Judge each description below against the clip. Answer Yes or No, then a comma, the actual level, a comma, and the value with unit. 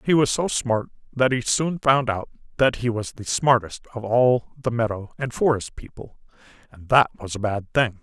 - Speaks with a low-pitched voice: Yes, low, 120 Hz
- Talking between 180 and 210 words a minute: Yes, average, 200 wpm